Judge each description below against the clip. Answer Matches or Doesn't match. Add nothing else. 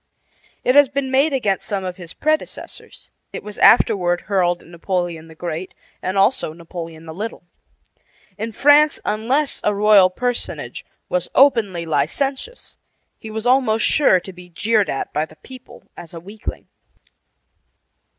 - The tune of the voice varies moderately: Doesn't match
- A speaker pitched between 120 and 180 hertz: Doesn't match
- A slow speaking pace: Doesn't match